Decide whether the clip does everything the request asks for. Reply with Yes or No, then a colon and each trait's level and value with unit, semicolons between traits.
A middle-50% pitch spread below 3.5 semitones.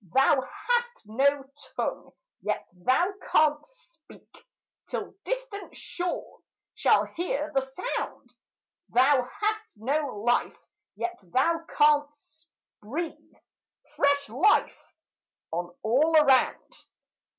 No: average, 5.2 semitones